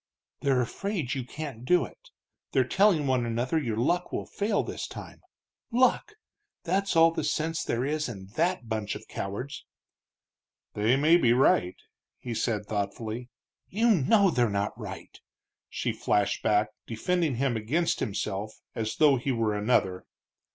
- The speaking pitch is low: Yes, low, 125 Hz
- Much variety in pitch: Yes, wide, 6.9 semitones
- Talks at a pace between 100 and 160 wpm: Yes, average, 150 wpm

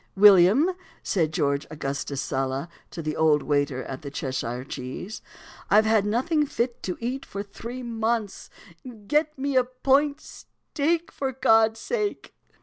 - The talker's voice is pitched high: Yes, high, 215 Hz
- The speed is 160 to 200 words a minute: No, average, 145 wpm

